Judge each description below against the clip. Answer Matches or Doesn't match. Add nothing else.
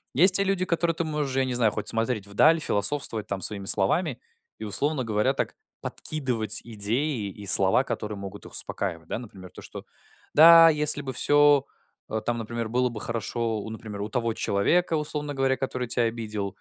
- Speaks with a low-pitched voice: Matches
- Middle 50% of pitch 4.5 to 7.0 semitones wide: Matches